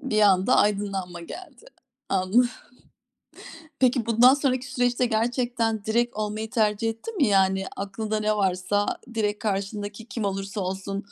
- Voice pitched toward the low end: No, high, 215 Hz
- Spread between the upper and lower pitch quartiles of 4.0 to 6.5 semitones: No, average, 3.4 semitones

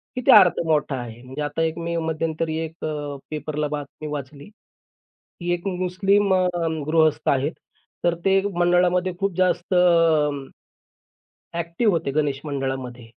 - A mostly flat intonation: No, average, 3.4 semitones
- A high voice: No, medium, 160 Hz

